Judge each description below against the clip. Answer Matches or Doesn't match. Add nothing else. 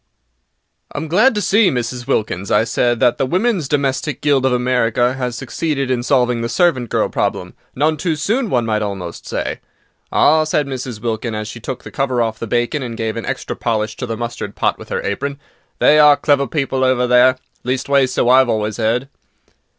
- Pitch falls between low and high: Doesn't match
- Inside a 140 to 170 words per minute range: Doesn't match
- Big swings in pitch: Doesn't match